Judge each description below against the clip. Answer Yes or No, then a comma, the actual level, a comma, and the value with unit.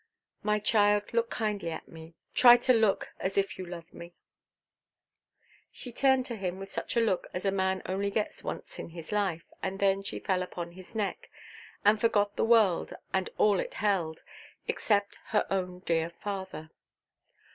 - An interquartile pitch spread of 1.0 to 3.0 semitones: Yes, average, 2.7 semitones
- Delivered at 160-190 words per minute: Yes, average, 175 wpm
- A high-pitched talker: Yes, high, 195 Hz